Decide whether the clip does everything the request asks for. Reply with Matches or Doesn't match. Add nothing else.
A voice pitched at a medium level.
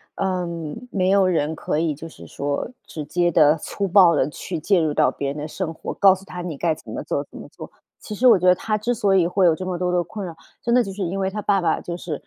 Matches